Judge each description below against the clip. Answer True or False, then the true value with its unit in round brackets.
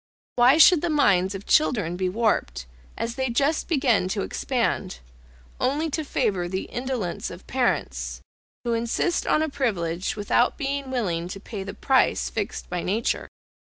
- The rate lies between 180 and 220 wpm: False (155 wpm)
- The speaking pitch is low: False (230 Hz)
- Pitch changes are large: True (6.3 semitones)